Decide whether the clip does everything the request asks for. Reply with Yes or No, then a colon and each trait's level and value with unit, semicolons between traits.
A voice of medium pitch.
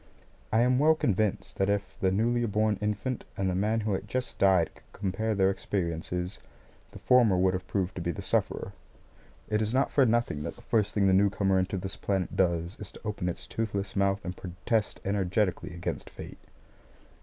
No: low, 100 Hz